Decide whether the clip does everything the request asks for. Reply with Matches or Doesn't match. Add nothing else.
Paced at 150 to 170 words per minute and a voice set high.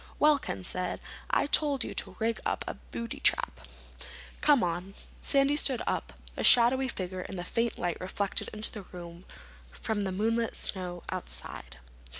Matches